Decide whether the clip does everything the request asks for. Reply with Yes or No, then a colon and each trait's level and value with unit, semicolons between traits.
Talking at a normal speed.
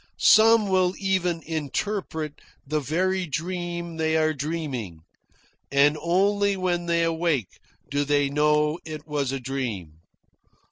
No: slow, 125 wpm